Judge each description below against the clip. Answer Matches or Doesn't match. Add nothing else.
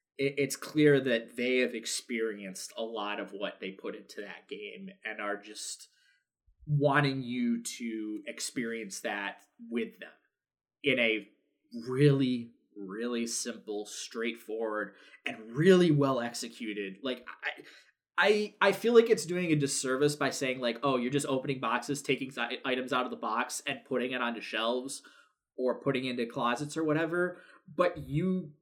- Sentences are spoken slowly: Doesn't match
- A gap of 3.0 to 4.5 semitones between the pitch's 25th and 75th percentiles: Matches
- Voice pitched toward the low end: Matches